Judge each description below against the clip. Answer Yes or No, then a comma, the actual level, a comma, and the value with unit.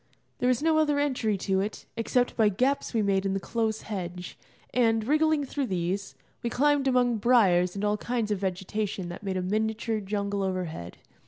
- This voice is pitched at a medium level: No, high, 215 Hz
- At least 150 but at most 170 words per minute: No, average, 185 wpm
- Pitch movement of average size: Yes, average, 4.5 semitones